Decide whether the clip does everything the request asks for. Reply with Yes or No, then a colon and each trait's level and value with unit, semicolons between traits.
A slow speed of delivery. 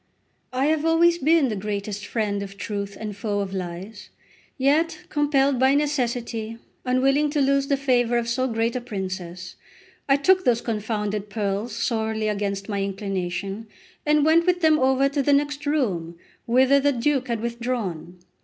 No: average, 165 wpm